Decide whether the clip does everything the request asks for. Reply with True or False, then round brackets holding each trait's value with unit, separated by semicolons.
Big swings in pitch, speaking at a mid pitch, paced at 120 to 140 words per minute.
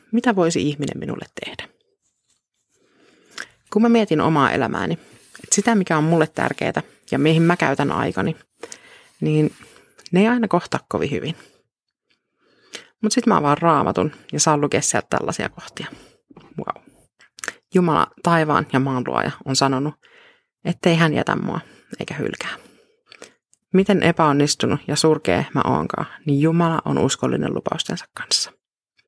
True (6.7 semitones; 165 Hz; 135 wpm)